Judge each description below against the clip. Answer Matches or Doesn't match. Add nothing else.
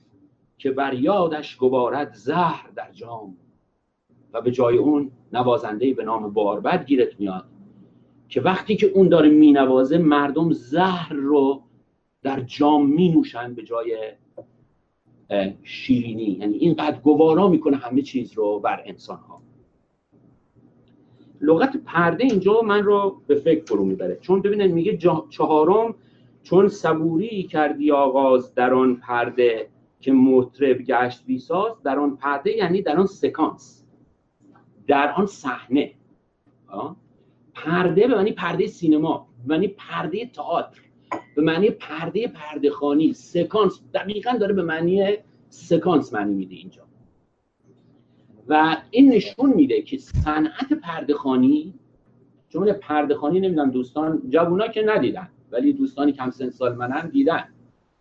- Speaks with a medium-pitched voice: Matches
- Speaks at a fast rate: Doesn't match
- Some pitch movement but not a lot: Doesn't match